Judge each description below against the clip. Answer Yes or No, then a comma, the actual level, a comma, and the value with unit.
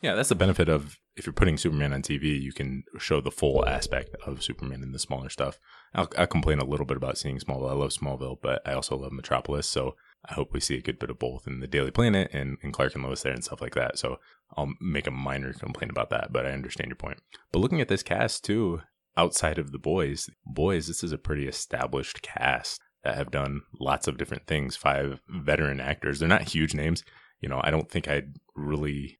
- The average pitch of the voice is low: Yes, very low, 70 Hz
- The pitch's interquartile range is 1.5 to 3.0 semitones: Yes, narrow, 2.5 semitones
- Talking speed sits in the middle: No, fast, 235 wpm